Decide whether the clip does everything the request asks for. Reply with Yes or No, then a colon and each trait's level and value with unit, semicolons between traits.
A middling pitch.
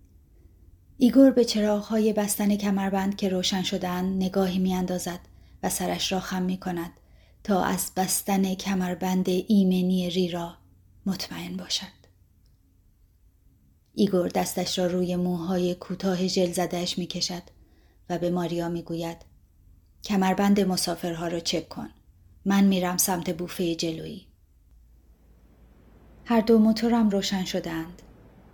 Yes: medium, 180 Hz